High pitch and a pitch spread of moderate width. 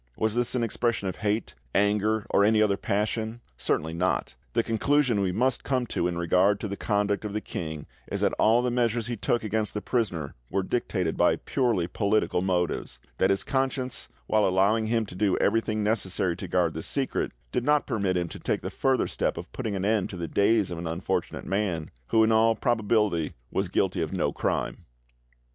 No: low, 105 Hz; average, 3.5 semitones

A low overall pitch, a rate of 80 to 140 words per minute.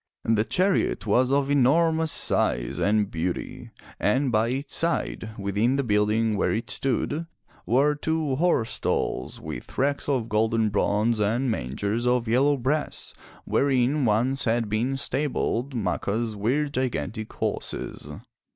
Yes: low, 120 Hz; slow, 135 wpm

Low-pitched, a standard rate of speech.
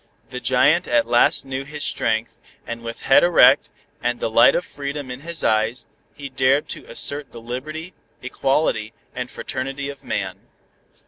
Yes: low, 130 Hz; average, 165 wpm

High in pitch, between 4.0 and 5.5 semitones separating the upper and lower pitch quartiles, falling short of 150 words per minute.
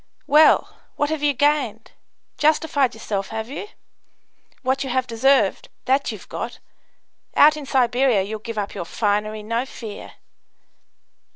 Yes: very high, 250 Hz; average, 4.5 semitones; slow, 135 wpm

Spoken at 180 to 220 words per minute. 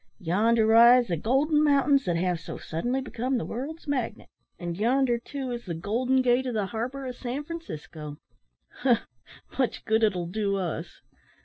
No: average, 170 wpm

